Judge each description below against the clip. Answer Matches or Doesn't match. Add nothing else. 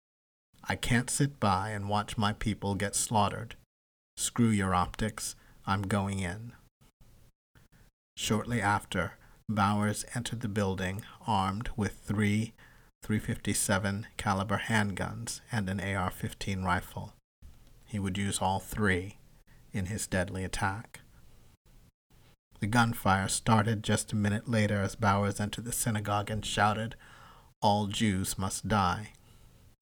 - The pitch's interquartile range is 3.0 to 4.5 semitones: Doesn't match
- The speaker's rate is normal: Doesn't match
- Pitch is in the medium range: Doesn't match